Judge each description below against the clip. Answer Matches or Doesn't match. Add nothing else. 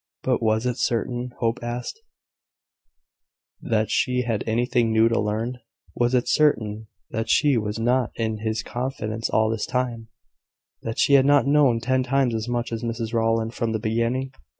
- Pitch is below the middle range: Matches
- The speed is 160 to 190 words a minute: Matches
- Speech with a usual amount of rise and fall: Doesn't match